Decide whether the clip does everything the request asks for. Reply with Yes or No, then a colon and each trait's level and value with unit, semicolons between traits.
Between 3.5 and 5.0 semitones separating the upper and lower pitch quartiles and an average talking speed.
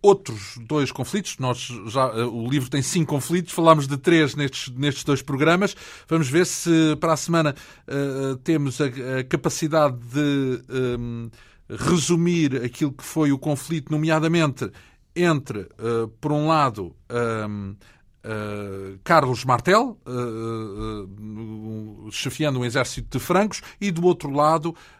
No: wide, 5.4 semitones; average, 135 wpm